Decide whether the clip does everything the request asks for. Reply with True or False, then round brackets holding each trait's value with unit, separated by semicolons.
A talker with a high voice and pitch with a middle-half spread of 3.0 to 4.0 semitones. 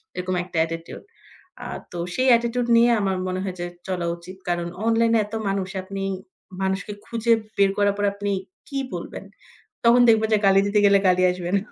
True (195 Hz; 3.7 semitones)